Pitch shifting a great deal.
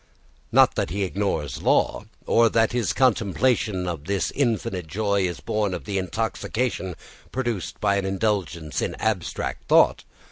No: average, 3.6 semitones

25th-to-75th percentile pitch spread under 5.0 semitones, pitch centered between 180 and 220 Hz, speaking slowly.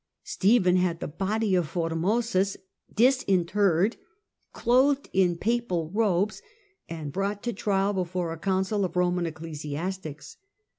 Yes: average, 3.6 semitones; medium, 185 Hz; slow, 115 wpm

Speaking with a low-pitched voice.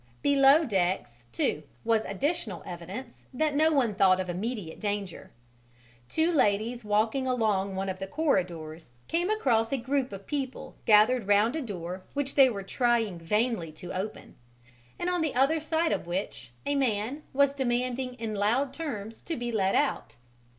No: high, 230 Hz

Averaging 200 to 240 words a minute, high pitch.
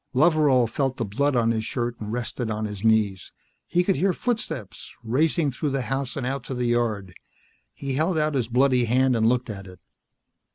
No: fast, 205 wpm; low, 125 Hz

